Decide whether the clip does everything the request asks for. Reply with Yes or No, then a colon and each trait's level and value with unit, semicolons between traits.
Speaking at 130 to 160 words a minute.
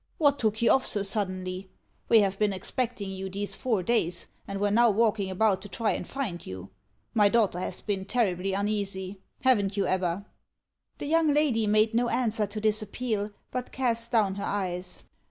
No: average, 185 wpm